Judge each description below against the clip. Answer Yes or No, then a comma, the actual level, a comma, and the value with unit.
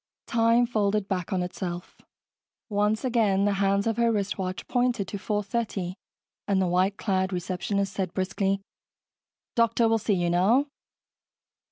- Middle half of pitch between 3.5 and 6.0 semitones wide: No, average, 3.1 semitones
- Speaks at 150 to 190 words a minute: No, average, 140 wpm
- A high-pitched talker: Yes, high, 200 Hz